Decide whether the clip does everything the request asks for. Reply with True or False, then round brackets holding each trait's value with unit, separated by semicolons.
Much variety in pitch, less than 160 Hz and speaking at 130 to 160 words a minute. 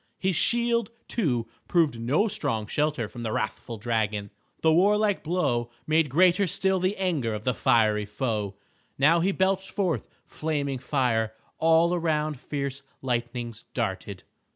True (7.4 semitones; 140 Hz; 140 wpm)